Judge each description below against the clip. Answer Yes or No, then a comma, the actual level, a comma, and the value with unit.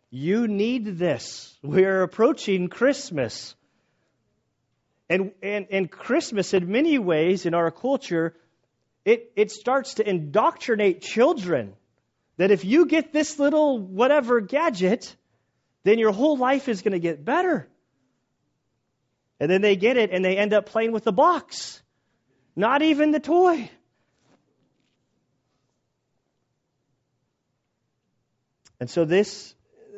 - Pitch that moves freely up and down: Yes, wide, 7.8 semitones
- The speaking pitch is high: Yes, high, 210 Hz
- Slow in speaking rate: Yes, slow, 120 wpm